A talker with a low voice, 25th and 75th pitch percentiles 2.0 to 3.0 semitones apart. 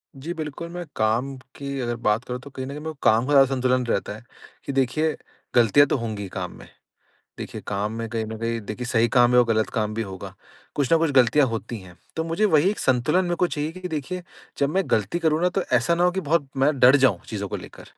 No: low, 130 Hz; average, 5.3 semitones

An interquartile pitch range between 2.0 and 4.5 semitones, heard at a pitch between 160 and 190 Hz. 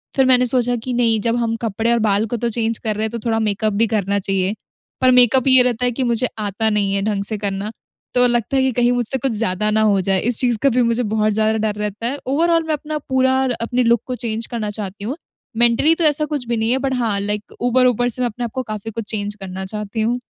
No: average, 2.8 semitones; high, 230 Hz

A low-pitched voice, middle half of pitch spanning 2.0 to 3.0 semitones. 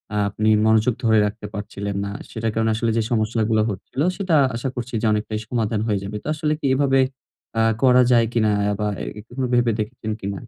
Yes: low, 110 Hz; narrow, 2.5 semitones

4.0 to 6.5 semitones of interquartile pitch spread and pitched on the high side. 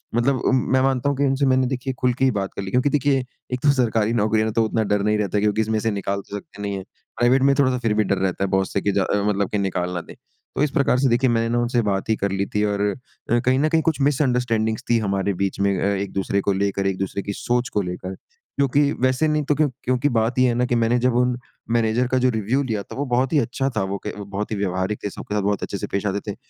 No: average, 4.3 semitones; low, 115 Hz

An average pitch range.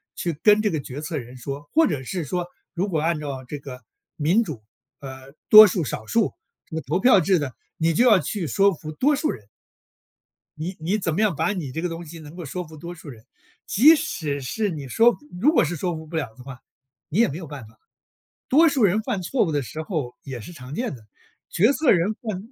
No: wide, 6.0 semitones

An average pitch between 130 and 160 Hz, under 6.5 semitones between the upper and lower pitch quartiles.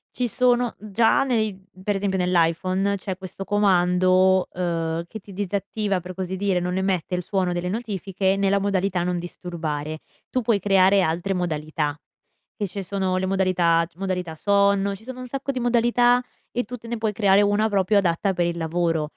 No: high, 190 Hz; narrow, 2.5 semitones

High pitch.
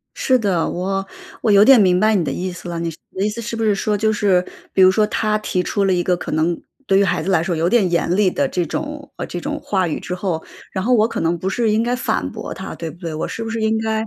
Yes: high, 195 Hz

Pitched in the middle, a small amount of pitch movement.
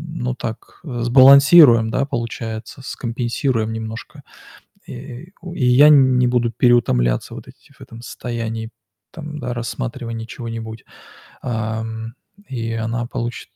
No: low, 120 Hz; narrow, 2.3 semitones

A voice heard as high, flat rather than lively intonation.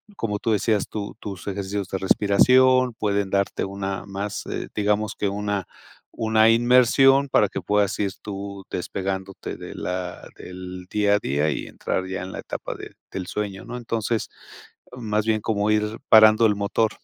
No: low, 105 Hz; narrow, 2.2 semitones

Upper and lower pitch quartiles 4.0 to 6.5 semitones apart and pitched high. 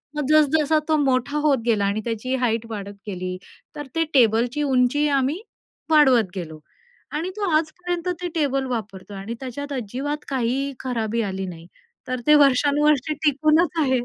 Yes: average, 4.9 semitones; very high, 260 Hz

